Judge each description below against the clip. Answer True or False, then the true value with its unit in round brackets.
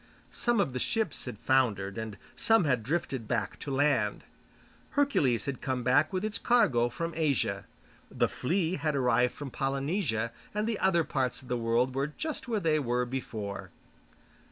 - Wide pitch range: True (5.8 semitones)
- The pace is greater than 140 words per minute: True (170 wpm)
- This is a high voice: False (135 Hz)